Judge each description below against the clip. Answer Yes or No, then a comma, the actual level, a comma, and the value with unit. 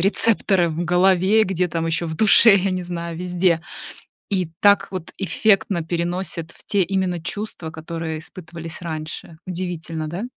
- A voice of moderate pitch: Yes, medium, 175 Hz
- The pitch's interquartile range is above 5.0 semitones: No, narrow, 2.5 semitones